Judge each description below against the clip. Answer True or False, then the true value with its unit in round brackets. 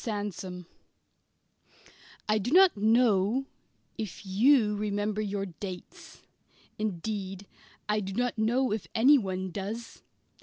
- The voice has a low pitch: False (210 Hz)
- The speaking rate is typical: False (105 wpm)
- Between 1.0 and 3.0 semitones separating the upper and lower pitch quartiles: True (2.7 semitones)